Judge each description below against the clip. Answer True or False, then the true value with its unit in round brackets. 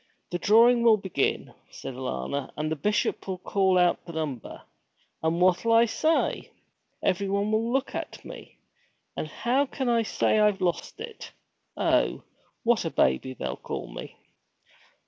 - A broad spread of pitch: True (6.3 semitones)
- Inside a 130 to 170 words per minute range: True (150 wpm)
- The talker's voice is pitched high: True (195 Hz)